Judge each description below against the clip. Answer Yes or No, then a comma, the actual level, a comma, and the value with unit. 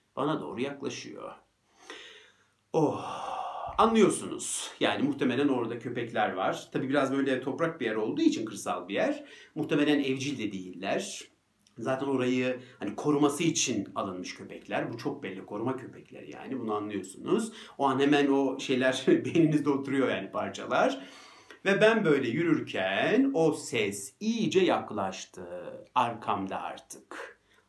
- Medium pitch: Yes, medium, 145 Hz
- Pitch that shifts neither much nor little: No, wide, 8.7 semitones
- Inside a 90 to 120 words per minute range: No, average, 130 wpm